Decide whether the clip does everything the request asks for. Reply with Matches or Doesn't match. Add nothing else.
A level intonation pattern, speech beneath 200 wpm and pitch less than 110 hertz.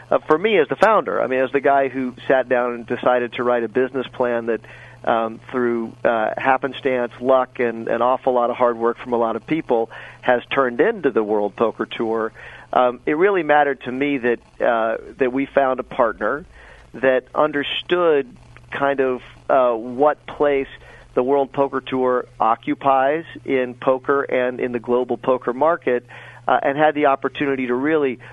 Doesn't match